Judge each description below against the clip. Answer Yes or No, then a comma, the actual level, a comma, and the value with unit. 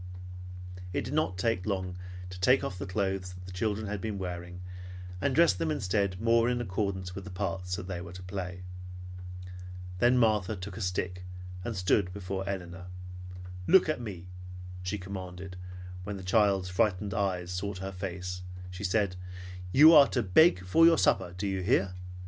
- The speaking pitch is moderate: No, very low, 95 Hz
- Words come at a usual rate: Yes, average, 170 wpm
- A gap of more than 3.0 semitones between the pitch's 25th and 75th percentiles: No, narrow, 2.4 semitones